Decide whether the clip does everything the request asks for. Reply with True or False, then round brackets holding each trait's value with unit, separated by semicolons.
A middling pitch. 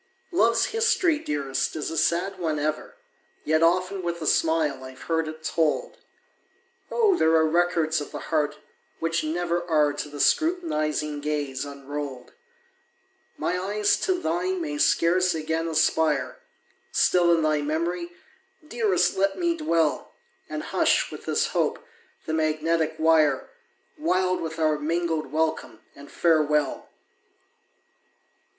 True (160 Hz)